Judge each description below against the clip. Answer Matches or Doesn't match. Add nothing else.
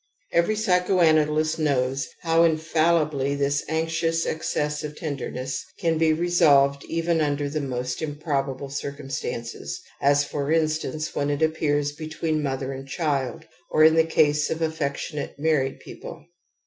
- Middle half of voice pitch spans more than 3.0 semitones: Doesn't match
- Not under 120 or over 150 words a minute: Matches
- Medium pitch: Matches